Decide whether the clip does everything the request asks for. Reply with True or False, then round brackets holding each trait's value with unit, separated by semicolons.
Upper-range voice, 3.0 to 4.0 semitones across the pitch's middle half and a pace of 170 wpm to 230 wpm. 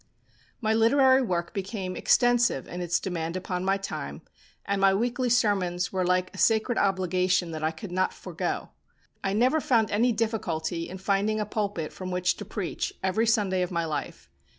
True (195 Hz; 3.5 semitones; 175 wpm)